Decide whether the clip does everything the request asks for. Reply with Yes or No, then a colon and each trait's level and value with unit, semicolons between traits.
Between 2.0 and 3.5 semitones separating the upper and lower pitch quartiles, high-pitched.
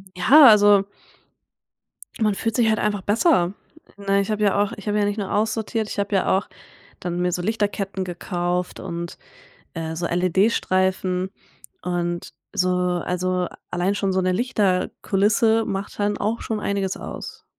Yes: narrow, 2.6 semitones; high, 195 Hz